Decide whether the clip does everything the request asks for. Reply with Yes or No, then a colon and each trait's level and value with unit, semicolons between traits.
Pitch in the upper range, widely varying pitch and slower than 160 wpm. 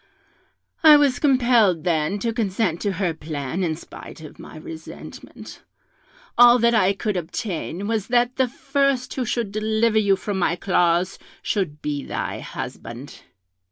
Yes: high, 200 Hz; wide, 6.2 semitones; average, 150 wpm